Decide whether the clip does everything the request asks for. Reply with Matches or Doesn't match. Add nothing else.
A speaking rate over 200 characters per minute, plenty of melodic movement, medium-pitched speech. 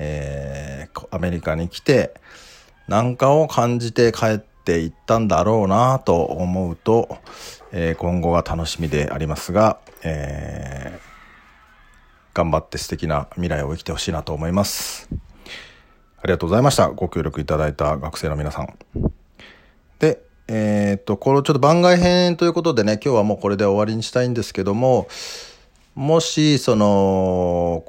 Doesn't match